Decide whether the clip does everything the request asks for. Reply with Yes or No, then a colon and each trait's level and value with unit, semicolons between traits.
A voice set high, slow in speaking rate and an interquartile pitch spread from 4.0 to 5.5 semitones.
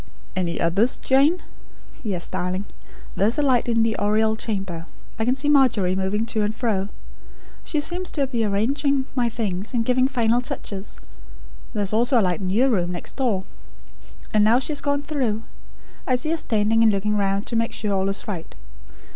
No: high, 220 Hz; average, 190 wpm; average, 4.4 semitones